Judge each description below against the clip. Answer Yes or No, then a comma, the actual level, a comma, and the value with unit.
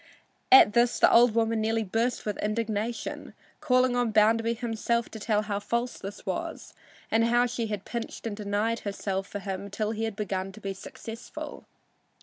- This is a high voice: Yes, high, 225 Hz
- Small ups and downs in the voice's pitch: Yes, narrow, 2.1 semitones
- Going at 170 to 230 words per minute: Yes, average, 175 wpm